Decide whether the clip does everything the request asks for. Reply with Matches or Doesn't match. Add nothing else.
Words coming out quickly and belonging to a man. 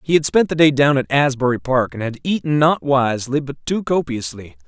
Matches